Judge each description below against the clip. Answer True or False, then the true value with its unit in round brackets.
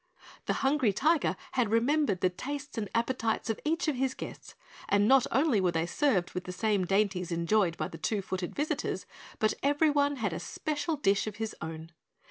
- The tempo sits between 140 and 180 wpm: False (195 wpm)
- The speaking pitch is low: False (220 Hz)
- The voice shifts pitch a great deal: True (7.5 semitones)